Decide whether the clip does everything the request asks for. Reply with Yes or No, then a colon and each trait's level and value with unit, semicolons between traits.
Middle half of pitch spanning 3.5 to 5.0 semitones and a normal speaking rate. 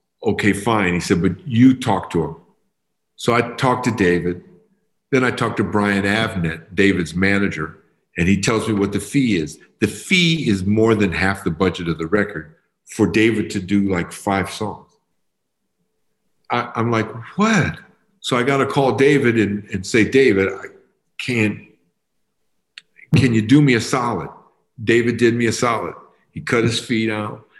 Yes: average, 3.8 semitones; average, 175 wpm